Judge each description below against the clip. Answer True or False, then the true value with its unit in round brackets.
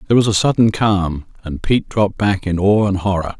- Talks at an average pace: False (230 wpm)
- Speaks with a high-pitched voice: False (100 Hz)